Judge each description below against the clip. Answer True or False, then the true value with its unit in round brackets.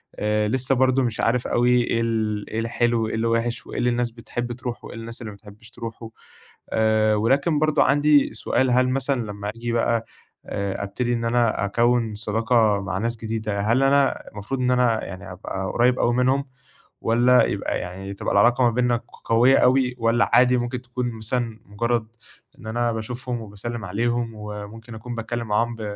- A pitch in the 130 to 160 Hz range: False (115 Hz)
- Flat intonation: True (2.0 semitones)